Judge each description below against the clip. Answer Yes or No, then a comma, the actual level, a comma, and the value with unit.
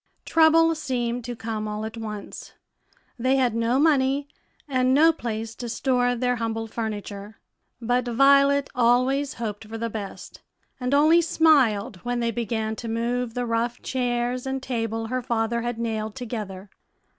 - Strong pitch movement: No, narrow, 2.6 semitones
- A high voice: Yes, high, 240 Hz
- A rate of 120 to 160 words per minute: Yes, average, 155 wpm